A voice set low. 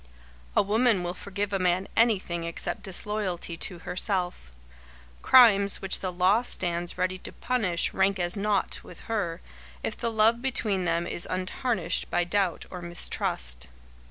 No: medium, 185 Hz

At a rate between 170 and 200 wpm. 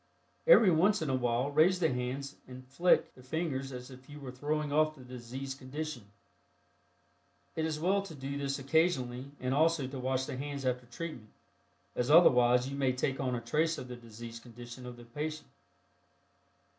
Yes: average, 180 wpm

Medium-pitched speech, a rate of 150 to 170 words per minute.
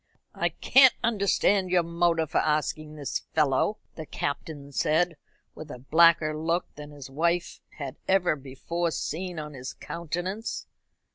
No: medium, 160 Hz; average, 140 wpm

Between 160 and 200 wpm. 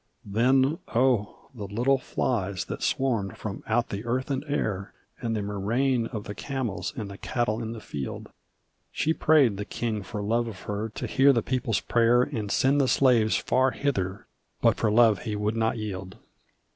Yes: average, 180 wpm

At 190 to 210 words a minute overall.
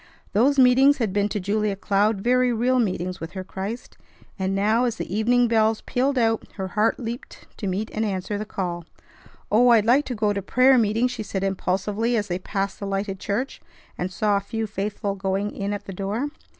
Yes: fast, 205 wpm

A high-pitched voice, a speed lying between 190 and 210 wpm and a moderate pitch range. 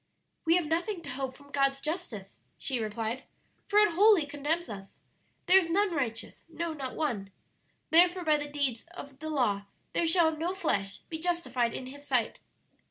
No: very high, 295 Hz; average, 175 wpm; average, 4.9 semitones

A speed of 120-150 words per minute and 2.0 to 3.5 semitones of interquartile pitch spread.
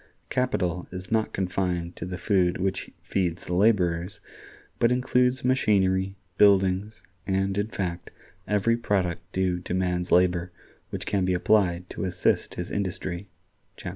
Yes: average, 140 wpm; narrow, 2.5 semitones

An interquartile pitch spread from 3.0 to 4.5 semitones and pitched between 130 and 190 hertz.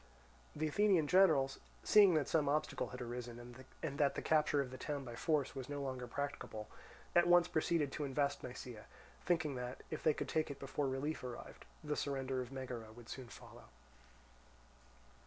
Yes: average, 3.4 semitones; medium, 140 Hz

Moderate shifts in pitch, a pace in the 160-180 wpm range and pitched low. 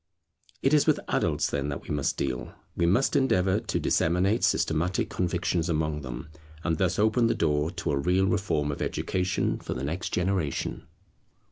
Yes: average, 4.4 semitones; average, 170 wpm; very low, 85 Hz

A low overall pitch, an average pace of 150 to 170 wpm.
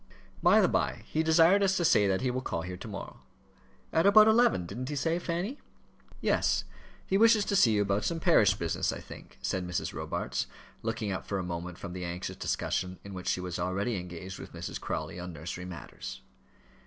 No: low, 100 Hz; fast, 205 wpm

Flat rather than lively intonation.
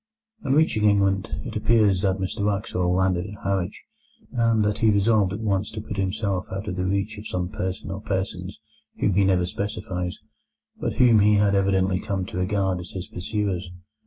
Yes: narrow, 2.0 semitones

